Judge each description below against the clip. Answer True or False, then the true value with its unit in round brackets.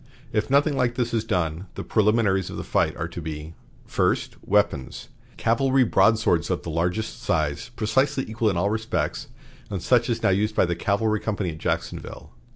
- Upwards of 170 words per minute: True (180 wpm)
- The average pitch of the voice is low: True (105 Hz)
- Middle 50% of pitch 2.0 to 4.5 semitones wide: False (4.9 semitones)